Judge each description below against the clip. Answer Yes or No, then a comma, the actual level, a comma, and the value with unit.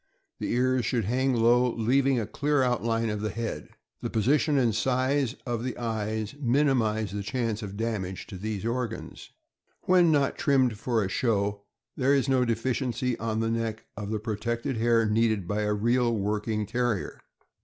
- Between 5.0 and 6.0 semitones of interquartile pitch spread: No, average, 2.9 semitones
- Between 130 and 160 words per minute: No, average, 175 wpm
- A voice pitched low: Yes, low, 115 Hz